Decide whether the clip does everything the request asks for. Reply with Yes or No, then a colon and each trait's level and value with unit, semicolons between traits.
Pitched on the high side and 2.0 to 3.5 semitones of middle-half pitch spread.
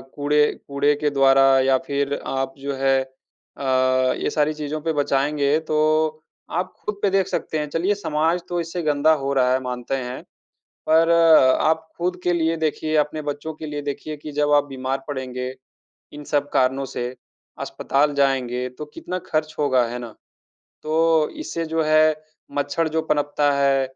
No: medium, 145 Hz; narrow, 2.6 semitones